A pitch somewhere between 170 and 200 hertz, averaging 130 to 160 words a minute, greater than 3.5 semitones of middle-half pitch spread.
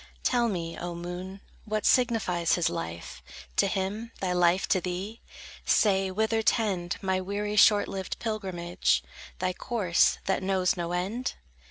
No: high, 190 Hz; average, 145 wpm; average, 3.1 semitones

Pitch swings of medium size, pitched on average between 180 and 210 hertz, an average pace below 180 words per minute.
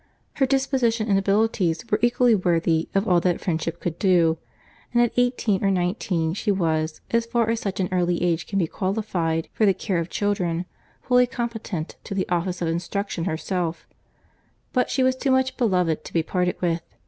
No: average, 4.8 semitones; high, 190 Hz; average, 185 wpm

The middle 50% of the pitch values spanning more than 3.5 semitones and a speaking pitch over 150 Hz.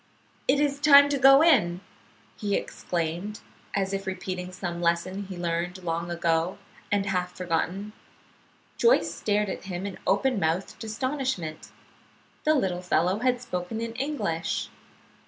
Yes: average, 5.2 semitones; high, 190 Hz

